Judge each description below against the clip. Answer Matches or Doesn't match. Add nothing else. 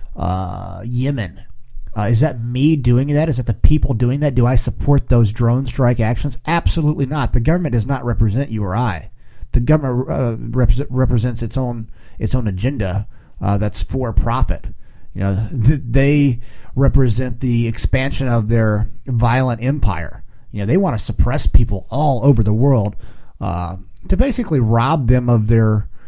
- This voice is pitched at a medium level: Doesn't match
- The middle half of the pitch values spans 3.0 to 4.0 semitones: Matches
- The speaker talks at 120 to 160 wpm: Doesn't match